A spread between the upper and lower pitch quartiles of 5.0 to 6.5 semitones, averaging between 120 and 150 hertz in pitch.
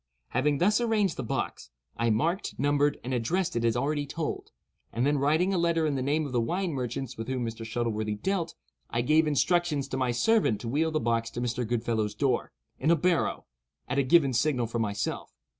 Yes: wide, 5.5 semitones; low, 135 Hz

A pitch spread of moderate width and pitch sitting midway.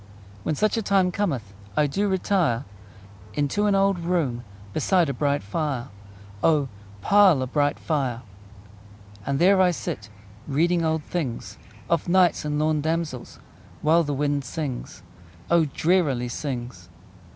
Yes: average, 4.7 semitones; medium, 150 Hz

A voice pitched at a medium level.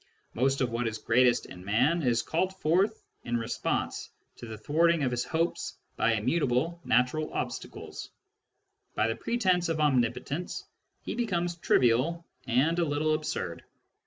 Yes: medium, 145 Hz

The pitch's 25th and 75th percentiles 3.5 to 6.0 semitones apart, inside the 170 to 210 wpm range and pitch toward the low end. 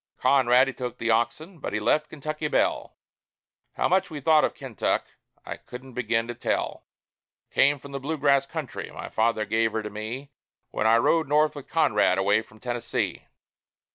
Yes: average, 4.4 semitones; average, 180 wpm; low, 130 Hz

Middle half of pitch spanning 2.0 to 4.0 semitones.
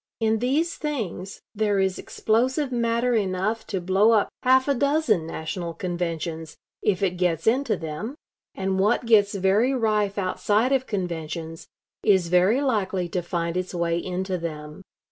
No: average, 4.6 semitones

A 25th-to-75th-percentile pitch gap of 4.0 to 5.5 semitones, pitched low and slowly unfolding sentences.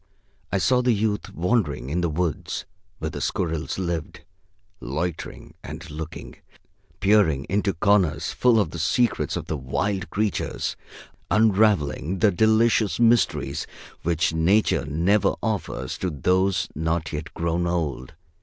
Yes: average, 4.8 semitones; very low, 90 Hz; slow, 130 wpm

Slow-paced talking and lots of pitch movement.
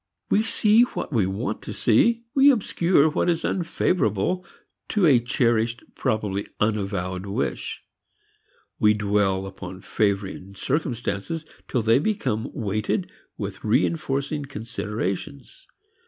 Yes: slow, 110 wpm; wide, 7.9 semitones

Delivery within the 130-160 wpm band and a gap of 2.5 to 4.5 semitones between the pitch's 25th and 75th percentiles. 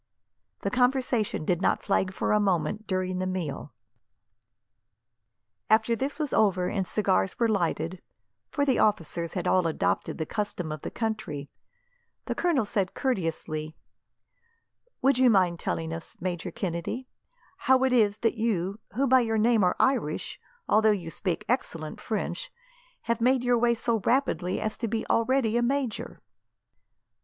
No: average, 150 wpm; average, 5.2 semitones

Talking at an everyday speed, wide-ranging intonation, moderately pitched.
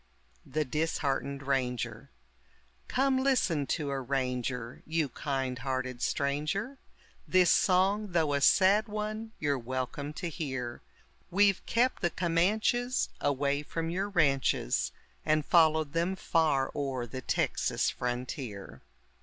No: slow, 120 wpm; wide, 5.7 semitones; medium, 150 Hz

